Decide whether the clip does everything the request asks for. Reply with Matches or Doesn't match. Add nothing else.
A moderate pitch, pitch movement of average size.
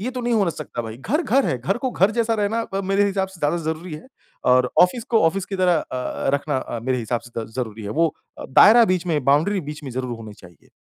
Doesn't match